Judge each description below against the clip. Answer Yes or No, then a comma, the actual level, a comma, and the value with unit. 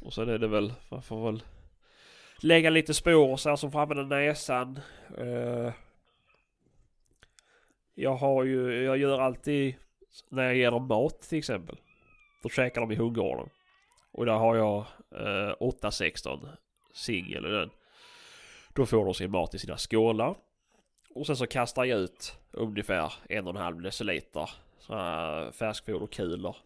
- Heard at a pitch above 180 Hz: No, low, 125 Hz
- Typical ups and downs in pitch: Yes, average, 3.9 semitones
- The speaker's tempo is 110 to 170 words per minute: Yes, average, 140 wpm